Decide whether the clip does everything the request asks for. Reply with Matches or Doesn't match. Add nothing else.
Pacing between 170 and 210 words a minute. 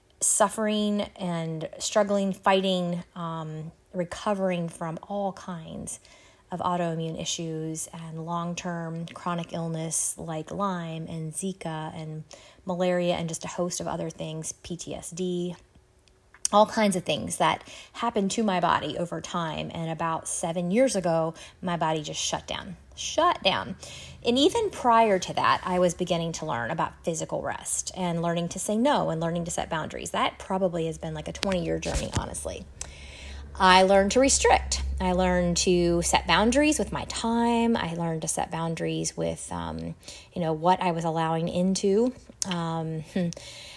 Doesn't match